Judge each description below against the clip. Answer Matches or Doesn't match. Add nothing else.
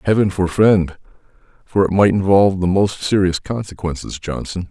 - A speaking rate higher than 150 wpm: Doesn't match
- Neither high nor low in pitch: Doesn't match